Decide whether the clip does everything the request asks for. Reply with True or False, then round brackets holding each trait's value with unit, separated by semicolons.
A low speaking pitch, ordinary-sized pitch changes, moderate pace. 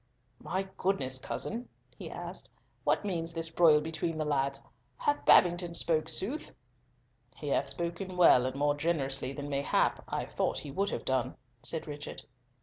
False (160 Hz; 3.5 semitones; 155 wpm)